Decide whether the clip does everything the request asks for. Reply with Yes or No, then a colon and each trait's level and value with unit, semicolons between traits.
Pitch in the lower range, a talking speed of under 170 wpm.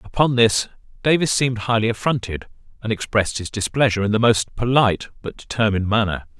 Yes: low, 110 Hz; average, 160 wpm